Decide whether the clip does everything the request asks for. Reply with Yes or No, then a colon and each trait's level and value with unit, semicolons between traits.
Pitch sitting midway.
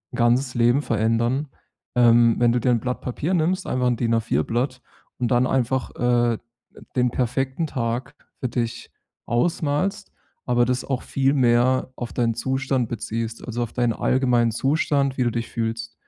No: low, 125 Hz